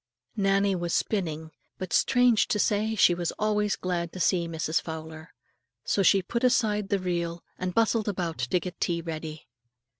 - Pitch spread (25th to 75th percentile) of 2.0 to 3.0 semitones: No, average, 3.7 semitones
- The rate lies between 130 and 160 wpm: No, average, 170 wpm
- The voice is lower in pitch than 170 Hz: No, medium, 185 Hz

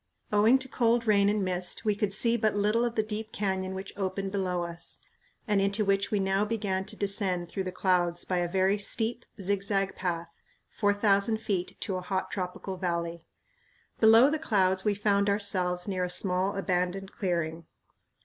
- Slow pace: No, average, 180 wpm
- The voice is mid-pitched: No, high, 195 Hz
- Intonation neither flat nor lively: No, narrow, 2.3 semitones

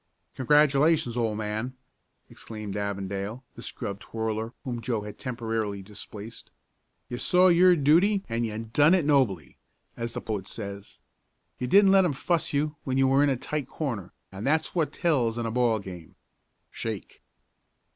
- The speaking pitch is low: Yes, low, 120 Hz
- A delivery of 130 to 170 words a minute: Yes, average, 160 wpm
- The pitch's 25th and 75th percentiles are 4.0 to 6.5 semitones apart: Yes, wide, 5.5 semitones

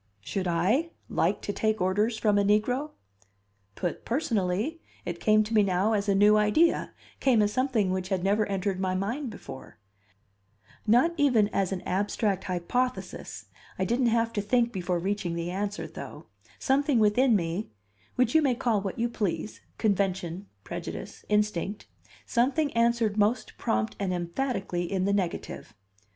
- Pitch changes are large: No, average, 3.9 semitones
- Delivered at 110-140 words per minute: No, average, 155 wpm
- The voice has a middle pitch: No, high, 210 Hz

